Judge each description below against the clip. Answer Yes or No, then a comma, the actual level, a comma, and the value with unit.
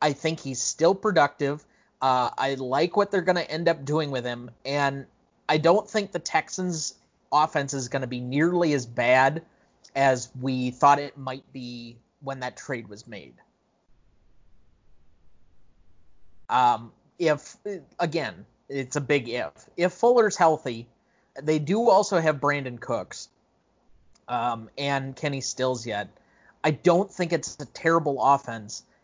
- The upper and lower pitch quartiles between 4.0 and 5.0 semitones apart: Yes, average, 4.6 semitones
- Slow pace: No, average, 145 wpm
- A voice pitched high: No, low, 135 Hz